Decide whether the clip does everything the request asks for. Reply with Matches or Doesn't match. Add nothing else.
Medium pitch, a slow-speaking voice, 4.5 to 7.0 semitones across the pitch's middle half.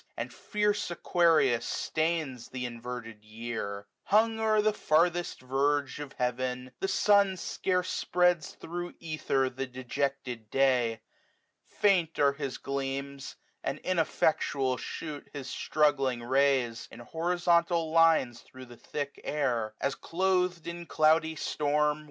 Matches